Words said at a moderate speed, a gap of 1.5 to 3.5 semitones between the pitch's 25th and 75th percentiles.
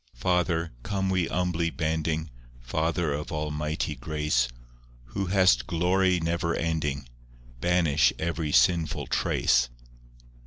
No: slow, 110 wpm; average, 2.8 semitones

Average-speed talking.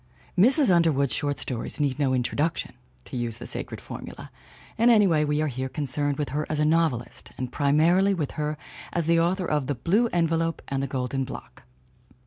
Yes: average, 190 wpm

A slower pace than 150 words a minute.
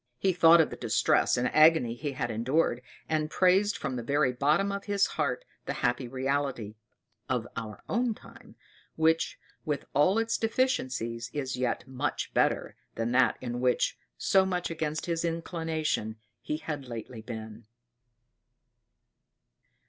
Yes: average, 140 wpm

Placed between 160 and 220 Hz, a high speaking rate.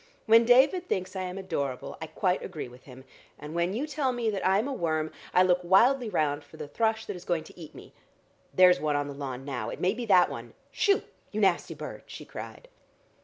Yes: medium, 185 Hz; fast, 230 wpm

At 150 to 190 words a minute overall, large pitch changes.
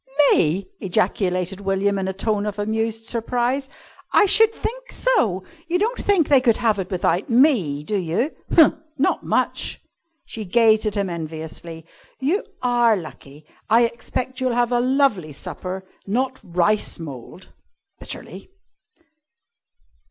No: slow, 135 wpm; wide, 5.8 semitones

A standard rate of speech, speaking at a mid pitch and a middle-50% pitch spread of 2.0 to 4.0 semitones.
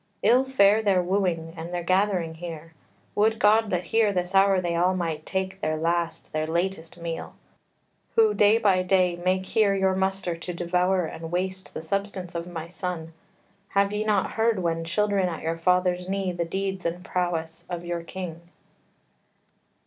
Yes: average, 170 wpm; medium, 180 Hz; narrow, 2.5 semitones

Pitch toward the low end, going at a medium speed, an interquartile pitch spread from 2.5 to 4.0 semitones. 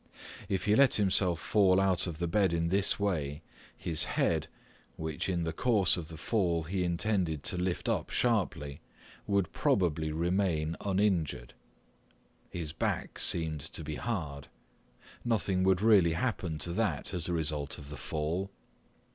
Yes: very low, 85 Hz; average, 155 wpm; average, 3.6 semitones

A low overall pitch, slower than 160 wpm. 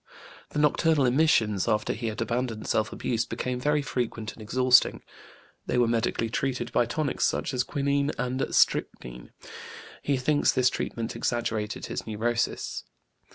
Yes: low, 120 Hz; average, 145 wpm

